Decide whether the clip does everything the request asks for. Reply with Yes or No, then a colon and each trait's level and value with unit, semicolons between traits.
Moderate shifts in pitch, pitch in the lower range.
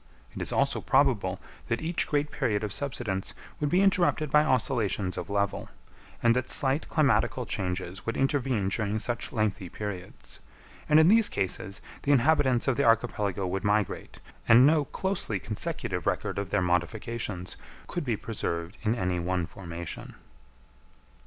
No: wide, 6.1 semitones; low, 115 Hz